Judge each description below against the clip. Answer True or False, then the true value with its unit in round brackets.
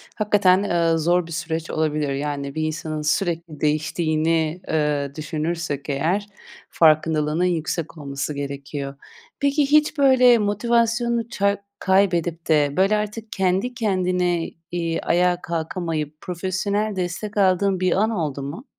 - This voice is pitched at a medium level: True (170 Hz)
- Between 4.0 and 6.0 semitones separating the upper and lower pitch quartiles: True (4.5 semitones)